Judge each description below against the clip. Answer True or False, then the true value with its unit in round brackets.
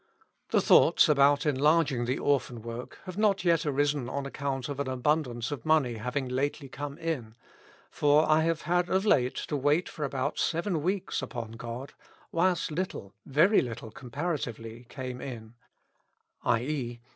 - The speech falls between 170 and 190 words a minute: False (160 wpm)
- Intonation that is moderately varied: True (4.1 semitones)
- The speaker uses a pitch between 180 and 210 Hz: False (140 Hz)